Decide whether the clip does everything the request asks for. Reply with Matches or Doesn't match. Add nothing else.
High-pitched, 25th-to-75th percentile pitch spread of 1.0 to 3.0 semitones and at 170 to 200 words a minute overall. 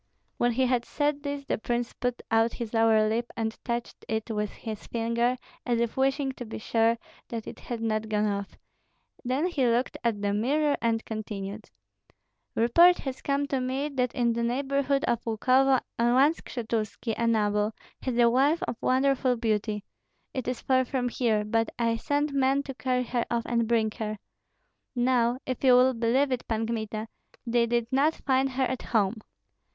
Matches